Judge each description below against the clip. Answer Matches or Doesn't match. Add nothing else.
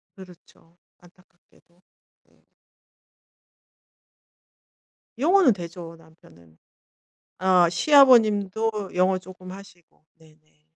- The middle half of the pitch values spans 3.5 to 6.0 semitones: Doesn't match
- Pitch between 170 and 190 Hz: Matches